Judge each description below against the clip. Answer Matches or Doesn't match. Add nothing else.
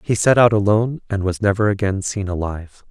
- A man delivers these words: Matches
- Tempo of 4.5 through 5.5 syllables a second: Doesn't match